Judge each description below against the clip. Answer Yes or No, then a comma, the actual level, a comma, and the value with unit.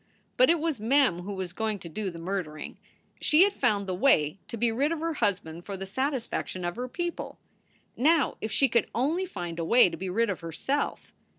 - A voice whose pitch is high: Yes, high, 220 Hz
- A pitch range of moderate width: No, wide, 7.1 semitones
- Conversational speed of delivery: No, fast, 220 wpm